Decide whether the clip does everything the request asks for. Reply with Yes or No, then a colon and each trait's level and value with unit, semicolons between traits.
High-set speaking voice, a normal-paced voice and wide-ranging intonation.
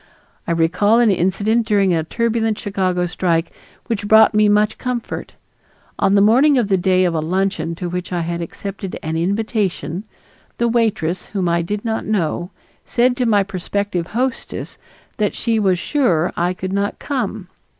No: high, 200 Hz; average, 170 wpm; average, 3.8 semitones